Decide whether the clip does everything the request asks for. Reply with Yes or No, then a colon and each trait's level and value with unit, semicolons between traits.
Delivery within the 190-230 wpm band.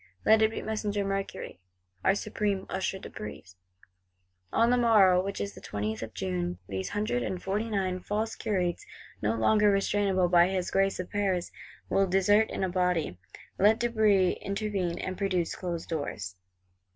No: average, 165 wpm